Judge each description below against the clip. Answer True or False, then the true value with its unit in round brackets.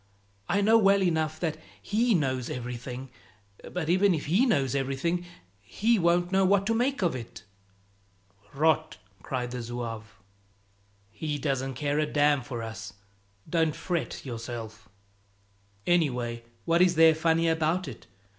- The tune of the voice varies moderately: False (5.8 semitones)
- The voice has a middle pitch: True (155 Hz)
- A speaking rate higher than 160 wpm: False (140 wpm)